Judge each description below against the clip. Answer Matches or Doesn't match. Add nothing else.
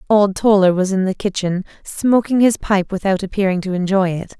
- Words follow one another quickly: Doesn't match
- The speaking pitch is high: Matches